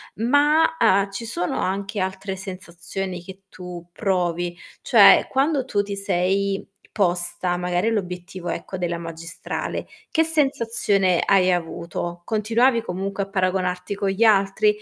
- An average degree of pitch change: Yes, average, 3.1 semitones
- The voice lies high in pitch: Yes, high, 195 Hz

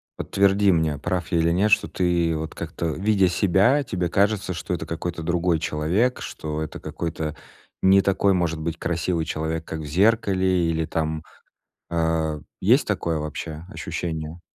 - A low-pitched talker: Yes, very low, 85 Hz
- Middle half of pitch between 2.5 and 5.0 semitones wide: Yes, average, 2.9 semitones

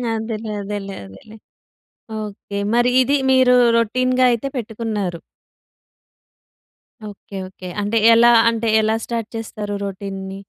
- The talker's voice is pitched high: Yes, high, 220 Hz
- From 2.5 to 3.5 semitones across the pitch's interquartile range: Yes, average, 2.8 semitones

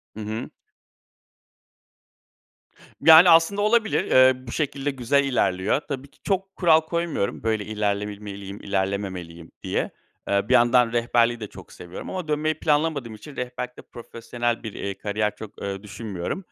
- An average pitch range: No, wide, 6.4 semitones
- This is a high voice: No, low, 120 Hz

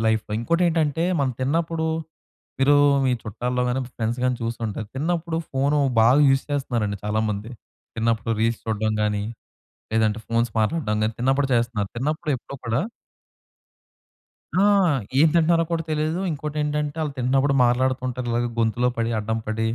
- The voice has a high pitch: No, low, 125 Hz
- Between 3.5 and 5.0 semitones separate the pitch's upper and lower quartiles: Yes, average, 4.7 semitones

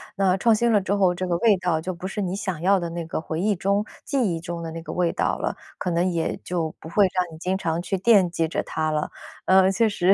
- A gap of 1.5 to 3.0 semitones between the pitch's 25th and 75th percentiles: Yes, average, 2.7 semitones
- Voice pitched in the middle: Yes, medium, 180 Hz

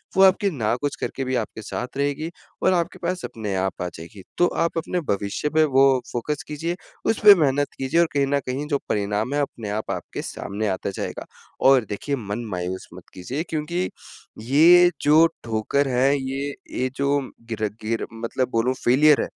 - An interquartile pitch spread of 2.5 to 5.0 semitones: No, wide, 5.6 semitones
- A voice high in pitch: No, low, 135 Hz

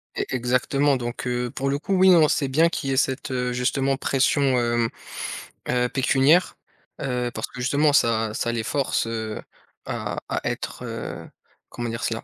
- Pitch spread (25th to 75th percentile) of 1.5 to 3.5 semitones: Yes, narrow, 2.6 semitones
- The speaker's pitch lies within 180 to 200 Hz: No, low, 130 Hz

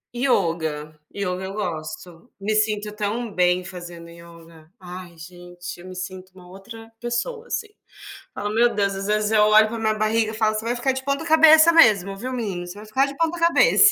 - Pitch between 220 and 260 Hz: No, high, 210 Hz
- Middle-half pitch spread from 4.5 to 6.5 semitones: Yes, average, 4.9 semitones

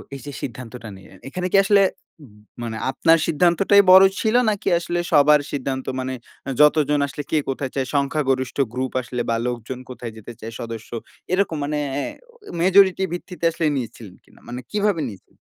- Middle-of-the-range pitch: Yes, medium, 145 Hz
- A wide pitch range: Yes, wide, 5.8 semitones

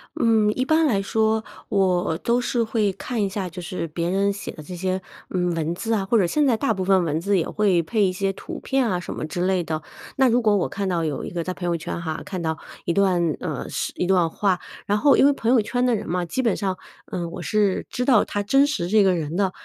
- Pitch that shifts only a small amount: No, average, 4.0 semitones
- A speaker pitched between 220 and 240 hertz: No, high, 195 Hz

